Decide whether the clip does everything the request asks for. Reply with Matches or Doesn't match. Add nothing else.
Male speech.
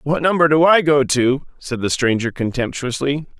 Matches